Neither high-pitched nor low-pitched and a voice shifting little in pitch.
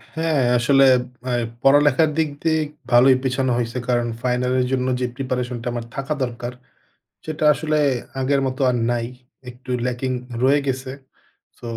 No: low, 130 Hz; narrow, 2.2 semitones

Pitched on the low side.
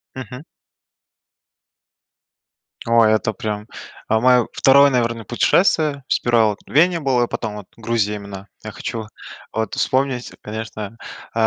Yes: low, 115 Hz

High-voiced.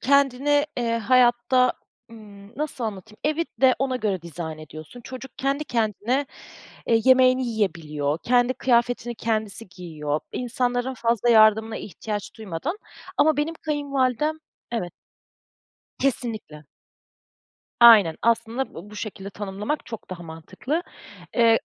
Yes: high, 230 Hz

